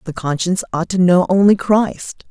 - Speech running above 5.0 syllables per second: No, 4.9 syllables/s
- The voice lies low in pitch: No, medium, 185 Hz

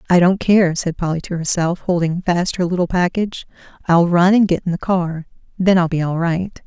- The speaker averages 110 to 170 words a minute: No, fast, 205 wpm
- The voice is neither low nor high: Yes, medium, 175 Hz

